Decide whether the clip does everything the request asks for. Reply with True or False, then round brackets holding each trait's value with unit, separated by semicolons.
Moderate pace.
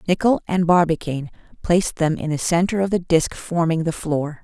True (190 wpm)